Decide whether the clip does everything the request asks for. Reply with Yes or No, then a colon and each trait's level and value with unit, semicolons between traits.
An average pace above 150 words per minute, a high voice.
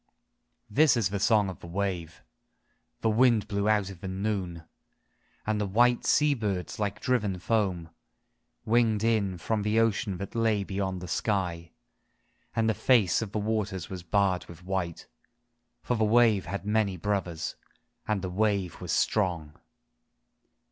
No: average, 160 wpm; low, 100 Hz